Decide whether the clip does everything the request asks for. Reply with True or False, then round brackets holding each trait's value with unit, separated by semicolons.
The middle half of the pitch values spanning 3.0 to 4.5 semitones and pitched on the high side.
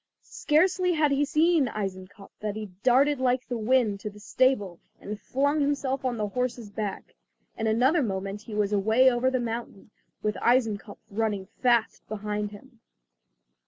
True (4.0 semitones; 230 Hz)